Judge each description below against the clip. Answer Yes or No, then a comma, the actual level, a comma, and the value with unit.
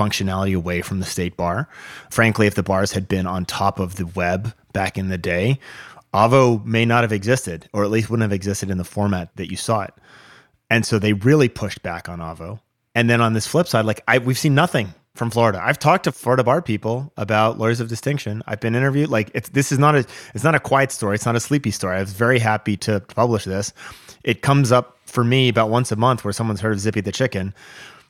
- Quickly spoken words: Yes, fast, 240 wpm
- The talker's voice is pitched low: Yes, low, 110 Hz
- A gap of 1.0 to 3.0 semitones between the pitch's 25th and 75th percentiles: No, average, 3.9 semitones